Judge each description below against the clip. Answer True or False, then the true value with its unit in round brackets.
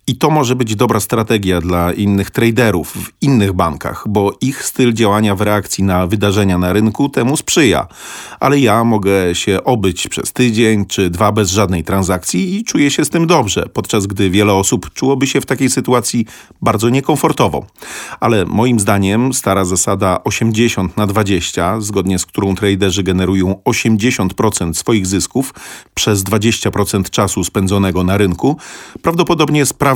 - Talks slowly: False (155 wpm)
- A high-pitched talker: False (105 Hz)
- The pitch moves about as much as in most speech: True (4.2 semitones)